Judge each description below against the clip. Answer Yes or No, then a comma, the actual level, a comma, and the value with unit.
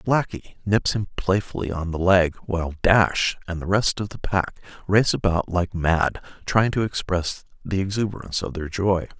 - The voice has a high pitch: No, very low, 95 Hz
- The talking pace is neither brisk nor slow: Yes, average, 175 wpm